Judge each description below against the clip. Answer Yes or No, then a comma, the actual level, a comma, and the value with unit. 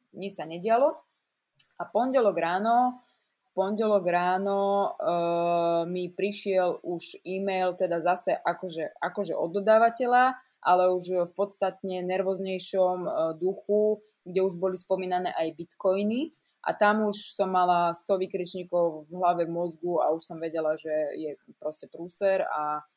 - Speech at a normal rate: Yes, average, 135 wpm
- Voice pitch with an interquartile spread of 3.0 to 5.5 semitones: No, narrow, 2.6 semitones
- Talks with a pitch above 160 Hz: Yes, medium, 185 Hz